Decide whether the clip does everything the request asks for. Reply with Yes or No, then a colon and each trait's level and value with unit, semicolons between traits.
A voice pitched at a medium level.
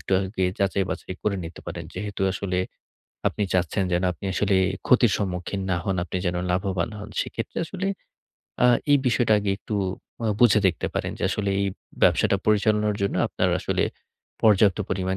No: low, 100 Hz